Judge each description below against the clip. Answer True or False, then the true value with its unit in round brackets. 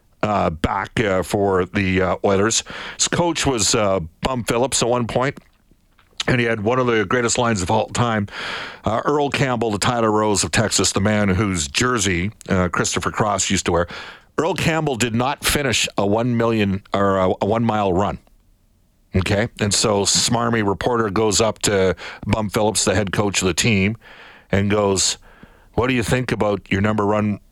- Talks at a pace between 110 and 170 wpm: False (185 wpm)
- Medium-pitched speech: False (105 Hz)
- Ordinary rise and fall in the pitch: True (3.3 semitones)